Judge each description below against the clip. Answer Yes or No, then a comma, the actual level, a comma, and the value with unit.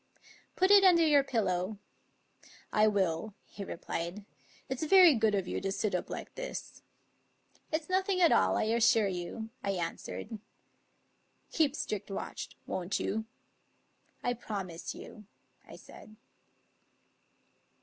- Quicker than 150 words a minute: No, average, 145 wpm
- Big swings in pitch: Yes, wide, 7.5 semitones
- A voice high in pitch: Yes, high, 215 Hz